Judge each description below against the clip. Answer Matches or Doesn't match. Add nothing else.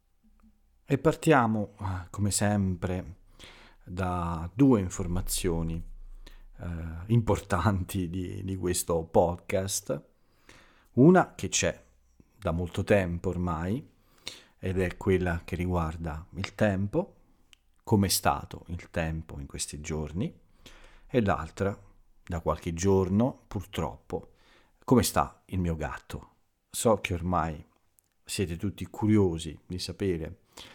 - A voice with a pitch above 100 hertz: Doesn't match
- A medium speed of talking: Doesn't match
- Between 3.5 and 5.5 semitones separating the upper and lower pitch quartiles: Doesn't match